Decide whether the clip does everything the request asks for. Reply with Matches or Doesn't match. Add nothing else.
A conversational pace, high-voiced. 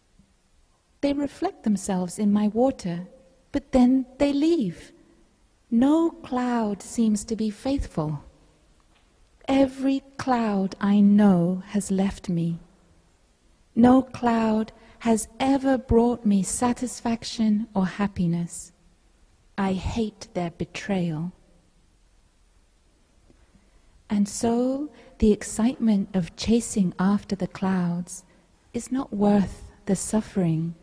Doesn't match